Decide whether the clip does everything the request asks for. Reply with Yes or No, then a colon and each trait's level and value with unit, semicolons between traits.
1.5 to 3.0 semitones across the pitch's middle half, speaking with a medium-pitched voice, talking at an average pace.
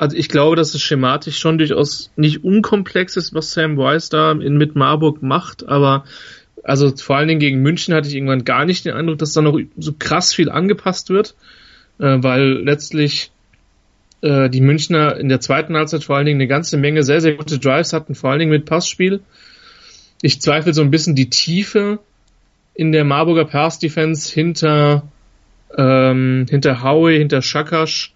Yes: narrow, 2.4 semitones; medium, 150 Hz; average, 175 wpm